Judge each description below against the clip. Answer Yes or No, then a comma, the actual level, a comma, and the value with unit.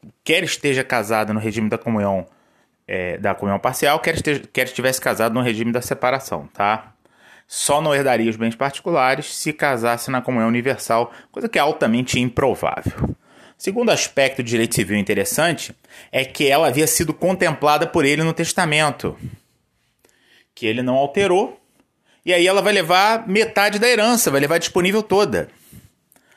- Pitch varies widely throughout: Yes, wide, 6.3 semitones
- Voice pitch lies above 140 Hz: No, low, 135 Hz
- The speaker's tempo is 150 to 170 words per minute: Yes, average, 155 wpm